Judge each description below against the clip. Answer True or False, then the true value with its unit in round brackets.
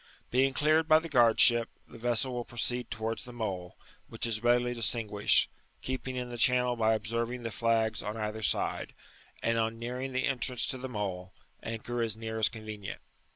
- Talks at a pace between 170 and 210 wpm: True (190 wpm)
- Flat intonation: True (2.0 semitones)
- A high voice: False (115 Hz)